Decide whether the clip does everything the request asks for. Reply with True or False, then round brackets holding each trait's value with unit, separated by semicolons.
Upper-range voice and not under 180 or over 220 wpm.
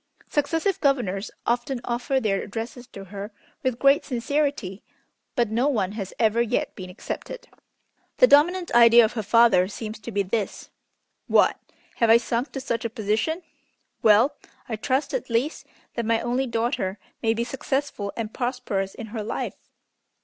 False (235 Hz; 160 wpm)